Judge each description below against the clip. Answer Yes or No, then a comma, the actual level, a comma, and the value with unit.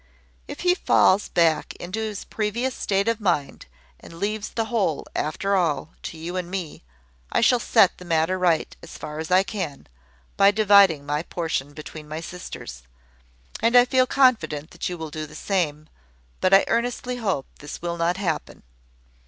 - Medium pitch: Yes, medium, 180 Hz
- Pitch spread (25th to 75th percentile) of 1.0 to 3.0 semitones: No, average, 4.9 semitones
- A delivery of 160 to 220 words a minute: Yes, average, 175 wpm